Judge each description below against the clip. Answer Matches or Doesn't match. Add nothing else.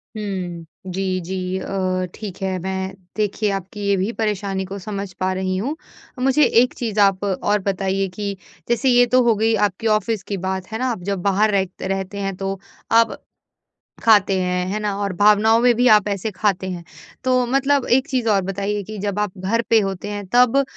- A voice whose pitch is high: Matches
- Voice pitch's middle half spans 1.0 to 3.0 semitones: Matches